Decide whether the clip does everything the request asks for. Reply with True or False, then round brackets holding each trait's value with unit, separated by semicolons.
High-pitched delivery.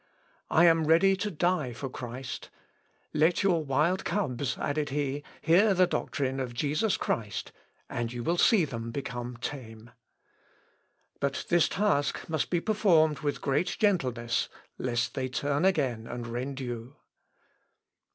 False (140 Hz)